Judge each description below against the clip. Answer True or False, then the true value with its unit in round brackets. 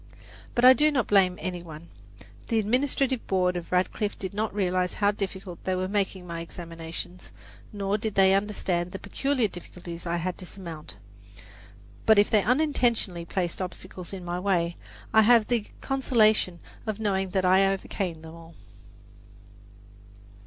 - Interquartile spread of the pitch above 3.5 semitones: False (3.2 semitones)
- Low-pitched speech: False (190 Hz)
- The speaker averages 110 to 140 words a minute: False (155 wpm)